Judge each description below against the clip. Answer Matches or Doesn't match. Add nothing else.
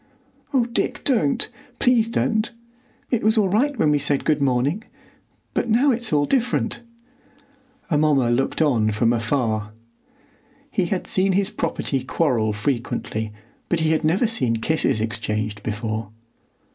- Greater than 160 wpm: Doesn't match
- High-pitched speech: Doesn't match